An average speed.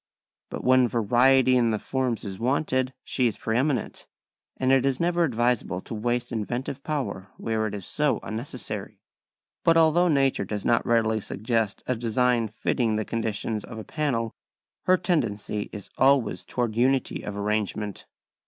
Yes: average, 160 wpm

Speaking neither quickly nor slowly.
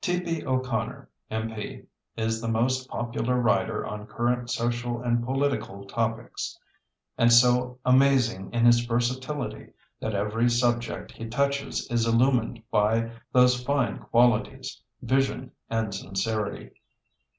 No: slow, 115 wpm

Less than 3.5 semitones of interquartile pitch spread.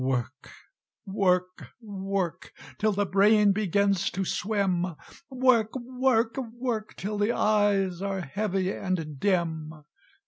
Yes: average, 2.9 semitones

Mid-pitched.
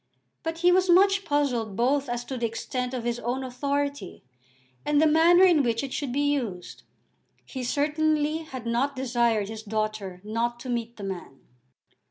No: very high, 255 Hz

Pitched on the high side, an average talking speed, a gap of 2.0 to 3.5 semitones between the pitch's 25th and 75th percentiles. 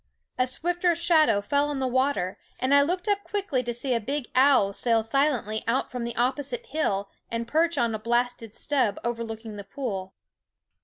No: very high, 255 Hz; average, 185 wpm; average, 4.3 semitones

